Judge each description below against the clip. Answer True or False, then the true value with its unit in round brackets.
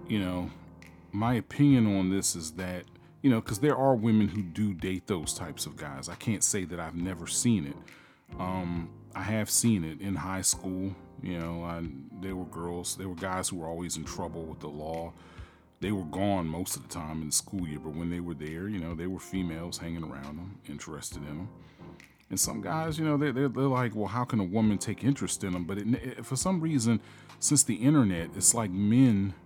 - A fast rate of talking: True (225 wpm)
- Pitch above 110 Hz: False (95 Hz)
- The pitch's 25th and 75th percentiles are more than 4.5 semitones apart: True (4.9 semitones)